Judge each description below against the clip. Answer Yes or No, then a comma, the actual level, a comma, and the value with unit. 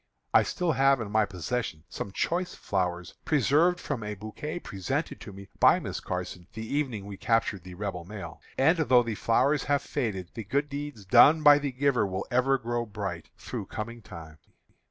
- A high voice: No, low, 115 Hz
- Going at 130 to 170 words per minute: No, average, 185 wpm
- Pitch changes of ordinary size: No, wide, 6.4 semitones